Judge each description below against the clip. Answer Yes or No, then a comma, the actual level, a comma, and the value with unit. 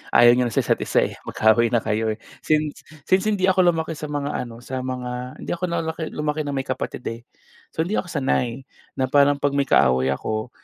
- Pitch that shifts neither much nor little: Yes, average, 4.6 semitones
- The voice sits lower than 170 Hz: Yes, low, 135 Hz